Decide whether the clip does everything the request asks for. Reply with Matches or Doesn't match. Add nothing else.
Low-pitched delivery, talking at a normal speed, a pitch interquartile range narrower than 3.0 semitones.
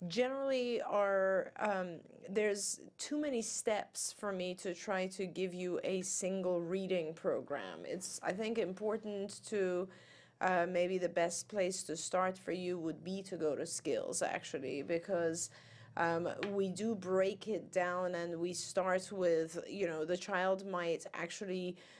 Doesn't match